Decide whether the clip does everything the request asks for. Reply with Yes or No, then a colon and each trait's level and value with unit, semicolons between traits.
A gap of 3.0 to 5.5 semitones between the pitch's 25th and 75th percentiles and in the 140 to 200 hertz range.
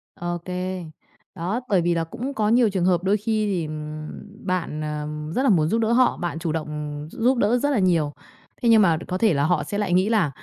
Yes: average, 4.8 semitones; medium, 185 Hz